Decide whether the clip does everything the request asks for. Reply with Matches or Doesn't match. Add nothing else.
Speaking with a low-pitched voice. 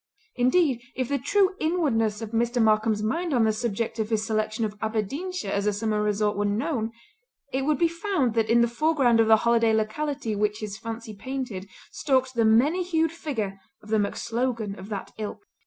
Doesn't match